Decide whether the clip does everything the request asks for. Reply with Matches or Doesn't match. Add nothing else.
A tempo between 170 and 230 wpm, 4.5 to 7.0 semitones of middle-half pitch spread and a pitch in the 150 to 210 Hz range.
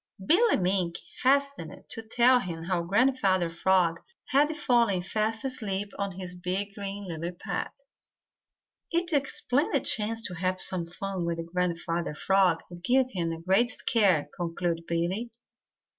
Doesn't match